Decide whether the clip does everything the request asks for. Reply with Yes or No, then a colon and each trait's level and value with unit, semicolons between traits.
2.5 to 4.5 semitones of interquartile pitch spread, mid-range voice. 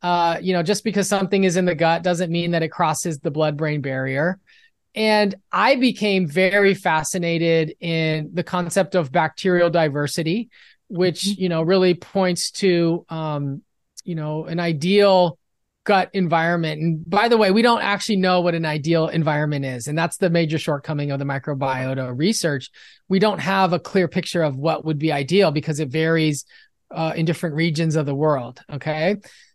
Yes: average, 3.2 semitones; medium, 170 Hz